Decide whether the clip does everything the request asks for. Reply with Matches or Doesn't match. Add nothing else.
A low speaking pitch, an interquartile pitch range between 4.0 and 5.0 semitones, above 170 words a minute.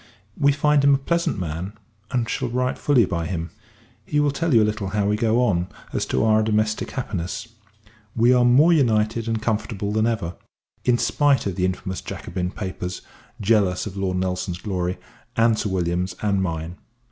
Matches